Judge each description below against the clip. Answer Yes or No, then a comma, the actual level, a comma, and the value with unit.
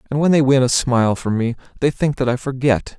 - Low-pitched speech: Yes, low, 130 Hz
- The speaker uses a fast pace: Yes, fast, 260 wpm